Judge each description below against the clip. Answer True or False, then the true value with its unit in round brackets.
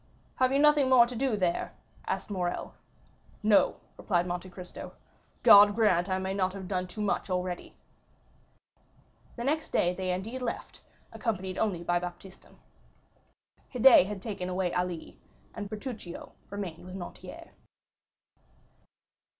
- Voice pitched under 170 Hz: False (190 Hz)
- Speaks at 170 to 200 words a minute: False (135 wpm)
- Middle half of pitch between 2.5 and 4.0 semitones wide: True (3.4 semitones)